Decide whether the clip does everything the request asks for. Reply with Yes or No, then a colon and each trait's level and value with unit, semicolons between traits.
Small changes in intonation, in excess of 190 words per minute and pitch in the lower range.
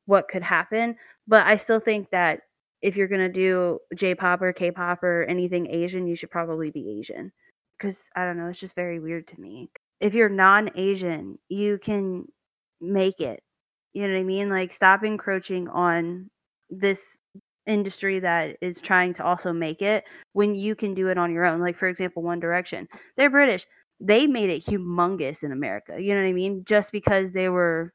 No: narrow, 2.2 semitones; average, 200 wpm; medium, 185 Hz